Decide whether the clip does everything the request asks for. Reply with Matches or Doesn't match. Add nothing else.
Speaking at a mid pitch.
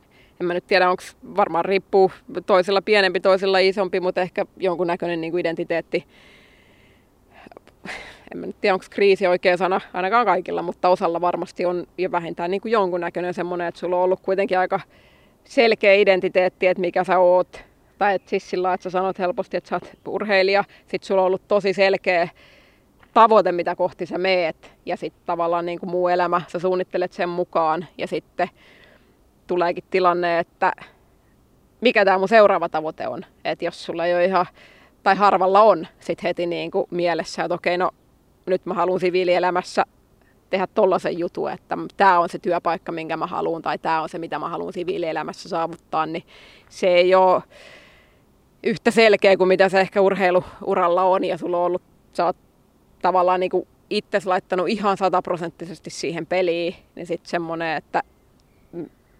Matches